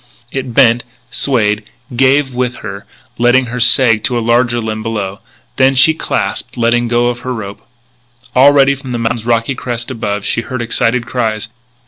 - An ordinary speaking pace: Yes, average, 160 wpm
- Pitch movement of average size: No, narrow, 2.1 semitones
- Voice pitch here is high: No, low, 120 Hz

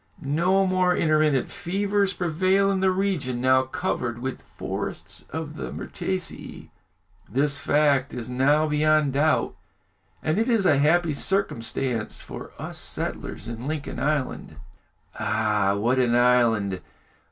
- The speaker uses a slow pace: Yes, slow, 130 wpm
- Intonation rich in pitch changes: Yes, wide, 6.1 semitones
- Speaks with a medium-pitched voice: Yes, medium, 150 Hz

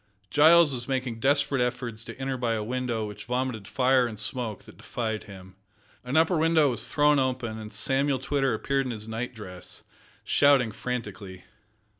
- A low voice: Yes, low, 125 Hz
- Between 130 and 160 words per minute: No, average, 170 wpm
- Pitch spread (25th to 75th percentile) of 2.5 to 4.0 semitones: Yes, average, 3.6 semitones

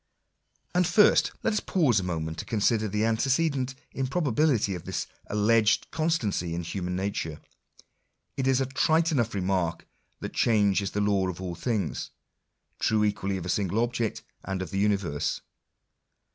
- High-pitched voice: No, low, 105 Hz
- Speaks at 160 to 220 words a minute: Yes, average, 165 wpm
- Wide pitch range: Yes, wide, 5.7 semitones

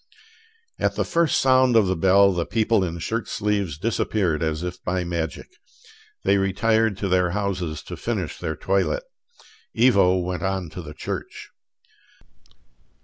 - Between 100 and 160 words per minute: Yes, average, 145 wpm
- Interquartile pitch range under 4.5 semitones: Yes, average, 3.3 semitones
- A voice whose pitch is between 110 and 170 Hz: No, very low, 95 Hz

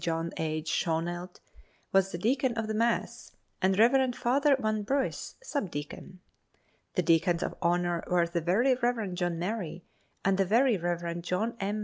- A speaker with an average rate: Yes, average, 160 wpm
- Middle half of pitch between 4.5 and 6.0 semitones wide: Yes, average, 5.1 semitones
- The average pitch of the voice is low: No, medium, 185 Hz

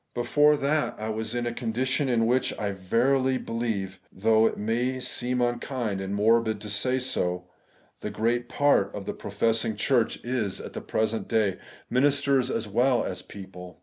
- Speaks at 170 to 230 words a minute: Yes, average, 175 wpm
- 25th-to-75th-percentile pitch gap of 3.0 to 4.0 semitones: Yes, average, 3.6 semitones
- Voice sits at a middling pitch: No, low, 115 Hz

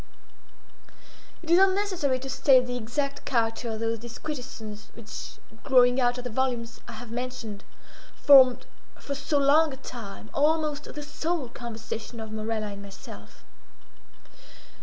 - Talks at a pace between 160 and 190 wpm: No, average, 140 wpm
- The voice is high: Yes, very high, 250 Hz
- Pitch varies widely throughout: No, average, 3.9 semitones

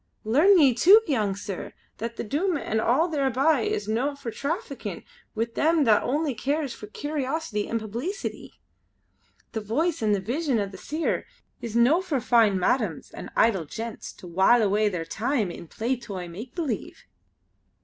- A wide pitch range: Yes, wide, 5.7 semitones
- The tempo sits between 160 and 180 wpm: Yes, average, 170 wpm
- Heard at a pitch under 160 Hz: No, high, 235 Hz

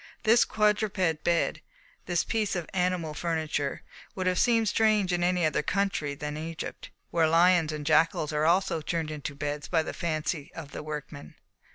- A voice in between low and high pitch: Yes, medium, 165 Hz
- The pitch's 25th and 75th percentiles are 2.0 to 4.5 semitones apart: Yes, average, 3.3 semitones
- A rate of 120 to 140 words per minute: No, average, 170 wpm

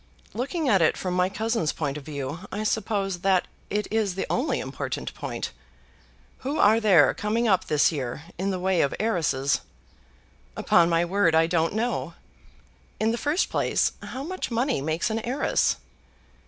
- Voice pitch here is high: Yes, high, 195 Hz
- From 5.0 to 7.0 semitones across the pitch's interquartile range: Yes, wide, 5.5 semitones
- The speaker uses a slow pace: No, average, 165 wpm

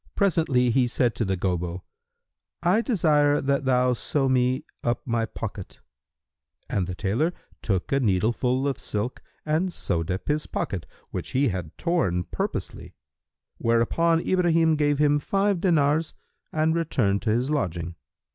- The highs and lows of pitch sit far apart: Yes, wide, 6.8 semitones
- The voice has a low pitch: Yes, low, 130 Hz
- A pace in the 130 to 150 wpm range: Yes, average, 145 wpm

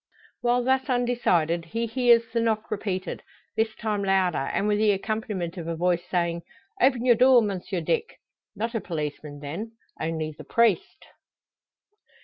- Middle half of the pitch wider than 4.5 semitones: Yes, average, 5.3 semitones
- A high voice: Yes, high, 210 Hz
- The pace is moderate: Yes, average, 150 wpm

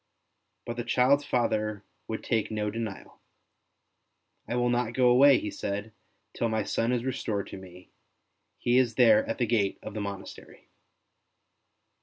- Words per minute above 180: No, average, 165 wpm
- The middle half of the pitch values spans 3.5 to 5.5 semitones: No, average, 2.8 semitones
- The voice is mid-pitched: No, low, 115 Hz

